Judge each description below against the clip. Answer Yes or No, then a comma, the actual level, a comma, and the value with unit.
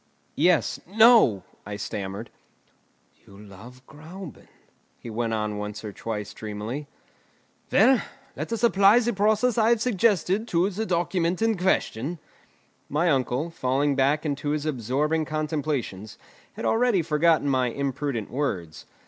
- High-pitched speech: No, medium, 150 Hz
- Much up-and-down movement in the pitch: Yes, wide, 8.3 semitones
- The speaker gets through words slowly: Yes, slow, 130 wpm